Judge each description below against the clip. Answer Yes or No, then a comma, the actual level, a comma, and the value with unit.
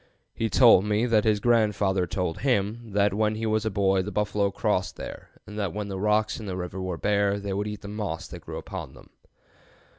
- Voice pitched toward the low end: Yes, low, 105 Hz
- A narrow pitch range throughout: Yes, narrow, 1.8 semitones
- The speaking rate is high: Yes, fast, 220 wpm